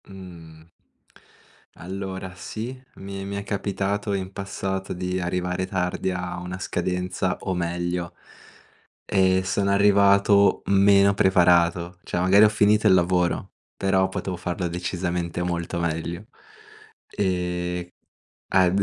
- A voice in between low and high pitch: No, very low, 95 Hz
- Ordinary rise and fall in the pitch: No, narrow, 1.8 semitones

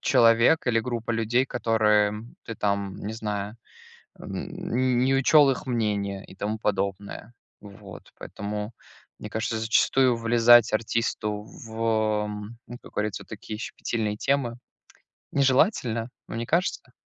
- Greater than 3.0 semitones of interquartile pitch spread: No, narrow, 2.4 semitones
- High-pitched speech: No, low, 115 Hz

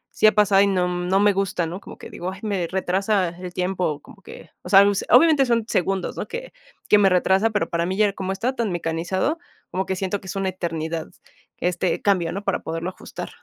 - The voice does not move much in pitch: Yes, narrow, 2.3 semitones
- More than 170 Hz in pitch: Yes, high, 190 Hz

